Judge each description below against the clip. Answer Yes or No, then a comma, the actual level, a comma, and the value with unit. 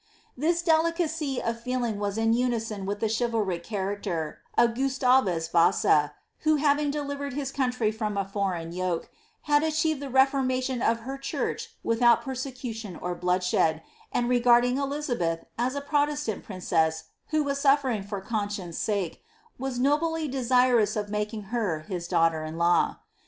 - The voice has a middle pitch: No, high, 235 Hz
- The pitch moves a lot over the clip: Yes, wide, 5.7 semitones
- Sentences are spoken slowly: No, average, 150 wpm